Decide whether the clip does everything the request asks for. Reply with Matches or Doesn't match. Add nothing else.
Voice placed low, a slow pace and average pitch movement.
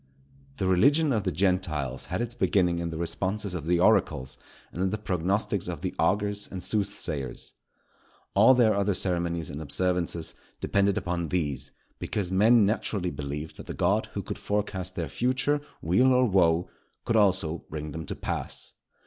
Doesn't match